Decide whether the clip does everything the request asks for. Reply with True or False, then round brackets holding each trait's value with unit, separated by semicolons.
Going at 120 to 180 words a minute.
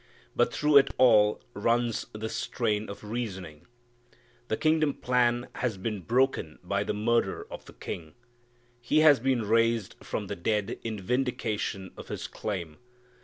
True (150 wpm)